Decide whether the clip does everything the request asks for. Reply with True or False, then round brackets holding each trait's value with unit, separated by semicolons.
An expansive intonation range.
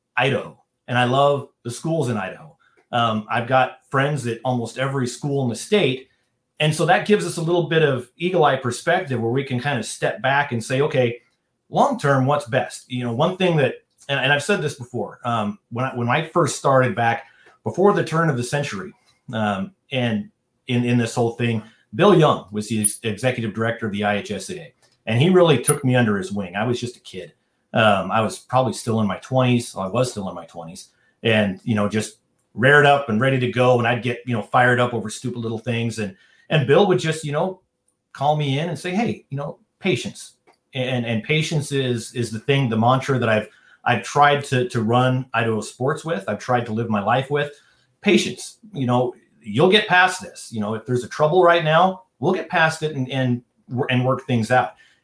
False (3.8 semitones)